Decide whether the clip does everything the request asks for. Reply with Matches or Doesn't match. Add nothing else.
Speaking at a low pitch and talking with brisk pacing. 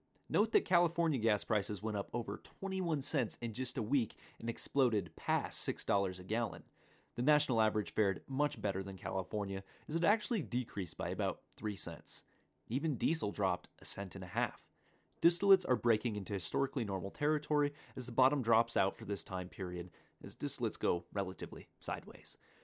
Doesn't match